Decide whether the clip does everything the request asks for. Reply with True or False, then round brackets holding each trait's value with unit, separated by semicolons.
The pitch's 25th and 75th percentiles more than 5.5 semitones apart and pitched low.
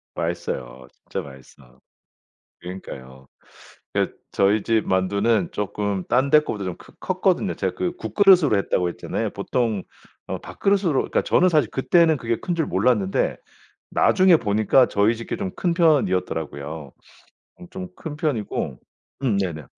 True (8.9 semitones; 105 Hz)